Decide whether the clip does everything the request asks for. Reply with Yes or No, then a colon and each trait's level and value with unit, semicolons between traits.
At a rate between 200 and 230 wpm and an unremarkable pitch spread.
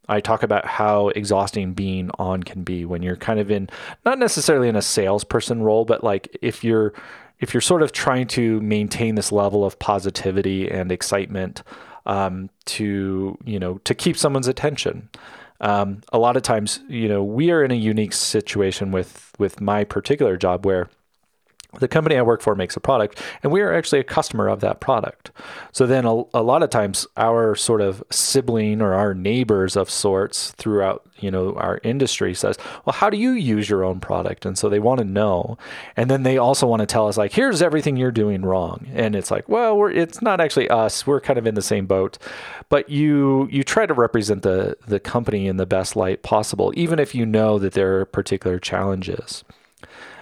Yes: fast, 205 wpm; average, 4.0 semitones